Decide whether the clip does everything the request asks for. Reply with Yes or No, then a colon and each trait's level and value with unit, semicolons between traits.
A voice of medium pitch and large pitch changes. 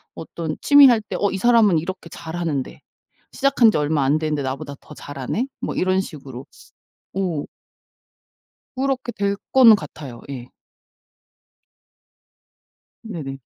Yes: medium, 170 Hz; wide, 7.1 semitones